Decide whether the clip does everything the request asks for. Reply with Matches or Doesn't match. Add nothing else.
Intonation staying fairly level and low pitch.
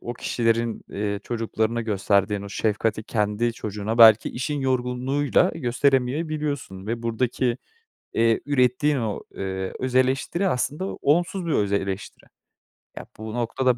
Doesn't match